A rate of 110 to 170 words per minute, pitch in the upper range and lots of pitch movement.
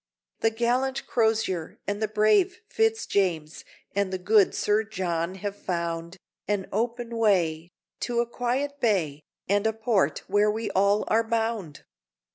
No: average, 140 wpm; high, 210 Hz; average, 3.6 semitones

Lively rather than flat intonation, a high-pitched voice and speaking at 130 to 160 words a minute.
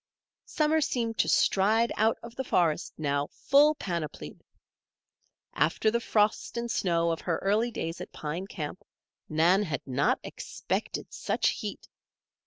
Yes: wide, 6.3 semitones; high, 195 Hz; average, 140 wpm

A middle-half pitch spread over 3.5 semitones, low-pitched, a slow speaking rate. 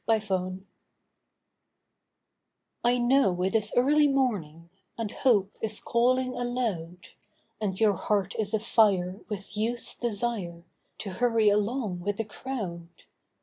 No: average, 4.2 semitones; high, 215 Hz; slow, 120 wpm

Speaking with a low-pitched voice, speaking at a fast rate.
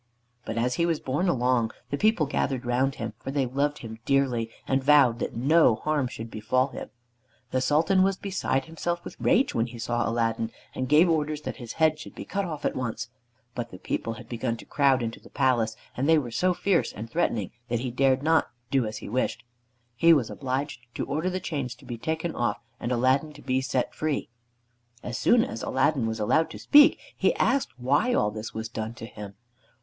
Yes: low, 130 Hz; fast, 215 wpm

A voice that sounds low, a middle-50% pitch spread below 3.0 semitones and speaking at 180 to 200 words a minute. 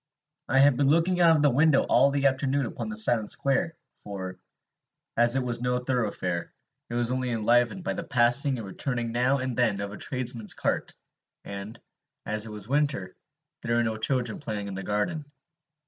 No: low, 125 Hz; average, 4.1 semitones; average, 190 wpm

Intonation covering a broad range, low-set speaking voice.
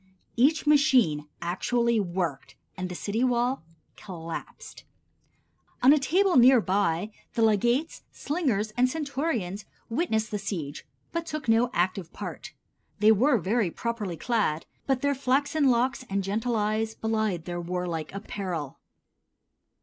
No: wide, 5.8 semitones; high, 220 Hz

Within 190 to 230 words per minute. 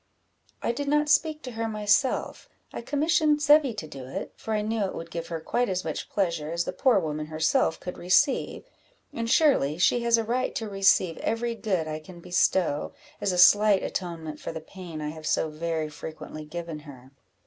Yes: average, 200 wpm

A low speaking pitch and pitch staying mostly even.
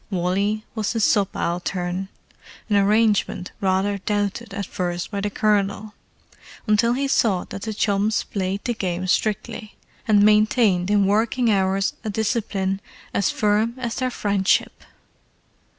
No: high, 205 Hz; narrow, 2.1 semitones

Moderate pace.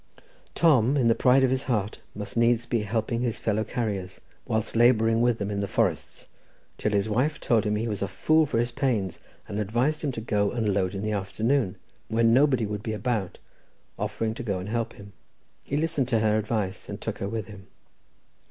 No: fast, 210 wpm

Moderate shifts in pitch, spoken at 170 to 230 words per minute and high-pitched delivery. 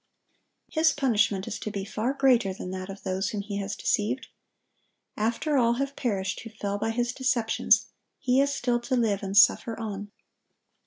Yes: average, 3.8 semitones; average, 175 wpm; high, 225 Hz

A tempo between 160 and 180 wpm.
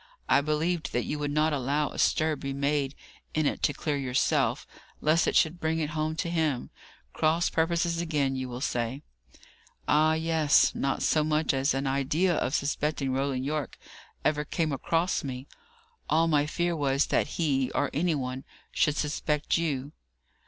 Yes: average, 170 wpm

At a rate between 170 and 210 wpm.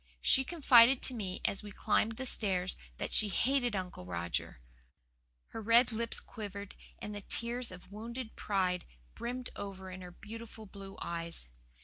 No: average, 155 wpm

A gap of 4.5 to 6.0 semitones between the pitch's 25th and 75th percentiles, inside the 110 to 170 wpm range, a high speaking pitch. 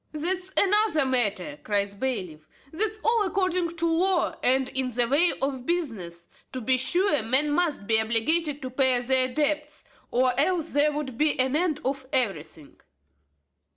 Yes: average, 5.2 semitones; average, 160 wpm; very high, 275 Hz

